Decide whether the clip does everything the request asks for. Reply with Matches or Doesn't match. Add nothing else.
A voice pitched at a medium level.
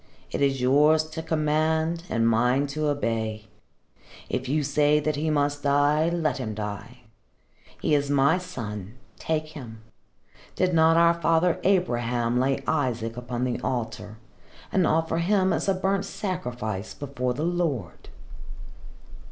Matches